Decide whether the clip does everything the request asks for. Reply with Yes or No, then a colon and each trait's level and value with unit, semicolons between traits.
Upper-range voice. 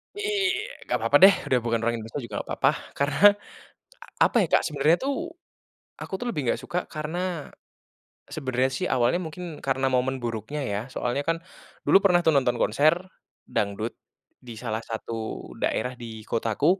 No: low, 135 Hz